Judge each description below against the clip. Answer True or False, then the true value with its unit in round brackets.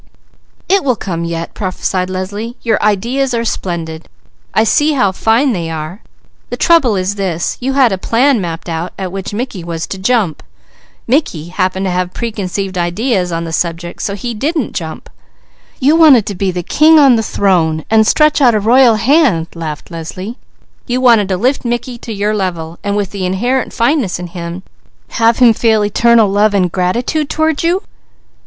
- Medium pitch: False (205 Hz)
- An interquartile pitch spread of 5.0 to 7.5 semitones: True (5.3 semitones)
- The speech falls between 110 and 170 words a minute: False (180 wpm)